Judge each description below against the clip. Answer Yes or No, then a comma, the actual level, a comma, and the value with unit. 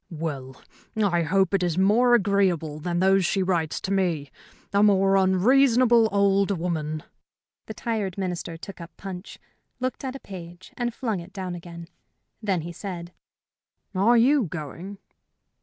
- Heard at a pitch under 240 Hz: Yes, high, 190 Hz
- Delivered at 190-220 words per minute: No, average, 155 wpm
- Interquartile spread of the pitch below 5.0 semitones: Yes, average, 3.1 semitones